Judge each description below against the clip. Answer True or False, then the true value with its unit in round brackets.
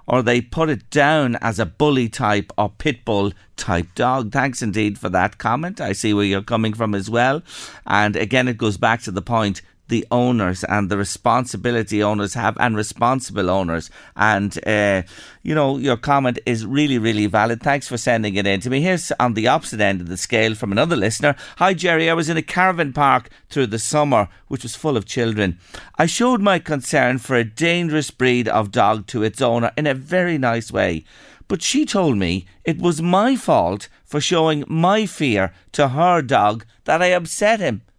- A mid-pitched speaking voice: False (120 Hz)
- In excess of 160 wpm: True (200 wpm)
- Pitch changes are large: True (6.1 semitones)